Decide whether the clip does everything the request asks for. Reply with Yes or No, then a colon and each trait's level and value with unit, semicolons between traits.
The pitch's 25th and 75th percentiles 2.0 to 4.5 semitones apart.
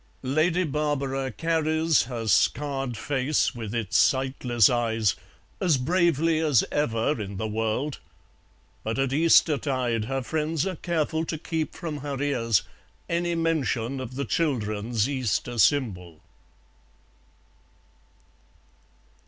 No: average, 5.1 semitones